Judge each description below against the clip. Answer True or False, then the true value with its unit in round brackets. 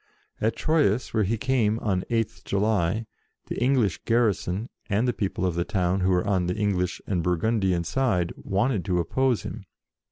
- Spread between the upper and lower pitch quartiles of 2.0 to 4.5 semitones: True (4.1 semitones)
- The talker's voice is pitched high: False (100 Hz)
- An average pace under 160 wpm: False (180 wpm)